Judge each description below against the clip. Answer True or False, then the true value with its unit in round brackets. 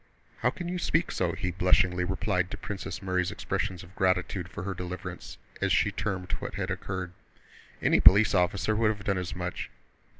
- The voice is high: False (95 Hz)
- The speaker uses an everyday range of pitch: False (1.9 semitones)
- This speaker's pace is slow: False (180 wpm)